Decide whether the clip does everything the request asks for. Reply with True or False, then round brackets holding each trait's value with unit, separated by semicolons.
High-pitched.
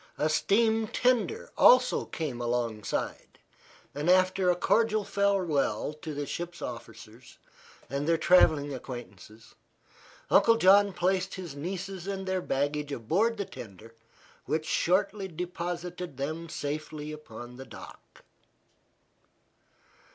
False (170 Hz)